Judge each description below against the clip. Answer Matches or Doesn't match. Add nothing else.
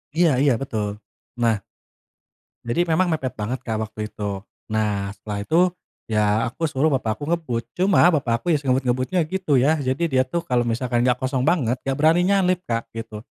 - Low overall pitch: Matches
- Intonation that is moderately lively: Doesn't match